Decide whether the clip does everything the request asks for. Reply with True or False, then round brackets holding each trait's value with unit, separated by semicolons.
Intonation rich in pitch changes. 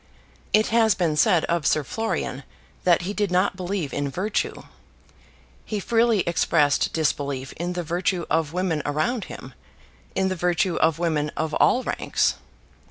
False (3.8 semitones)